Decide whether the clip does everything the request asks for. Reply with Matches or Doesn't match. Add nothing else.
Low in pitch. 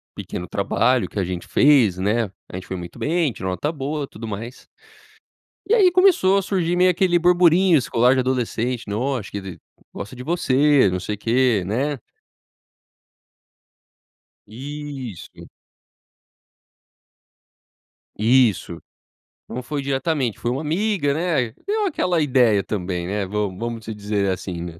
Matches